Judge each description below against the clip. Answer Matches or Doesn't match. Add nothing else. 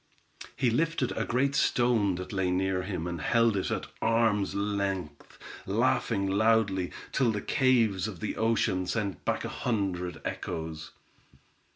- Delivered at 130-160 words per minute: Matches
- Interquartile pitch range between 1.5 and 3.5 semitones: Doesn't match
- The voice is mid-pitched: Doesn't match